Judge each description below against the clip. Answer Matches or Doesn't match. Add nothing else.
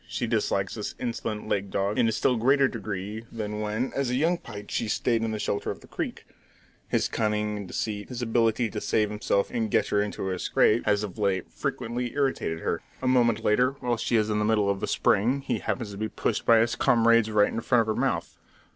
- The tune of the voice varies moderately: Doesn't match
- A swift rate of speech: Matches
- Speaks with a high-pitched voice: Doesn't match